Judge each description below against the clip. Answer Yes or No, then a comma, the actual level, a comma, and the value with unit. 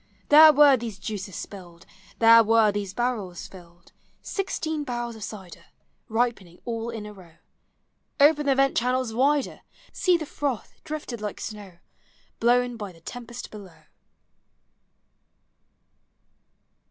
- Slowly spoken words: Yes, slow, 125 wpm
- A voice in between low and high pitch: No, high, 230 Hz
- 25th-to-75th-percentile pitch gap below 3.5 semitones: No, average, 4.6 semitones